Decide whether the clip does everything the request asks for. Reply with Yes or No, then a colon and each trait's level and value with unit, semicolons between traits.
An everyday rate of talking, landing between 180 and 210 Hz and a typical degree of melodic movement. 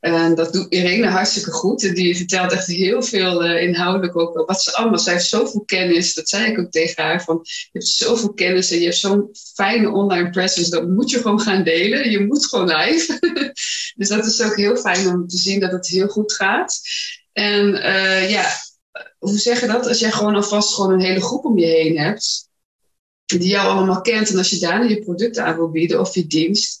No: fast, 220 wpm; high, 190 Hz; average, 3.4 semitones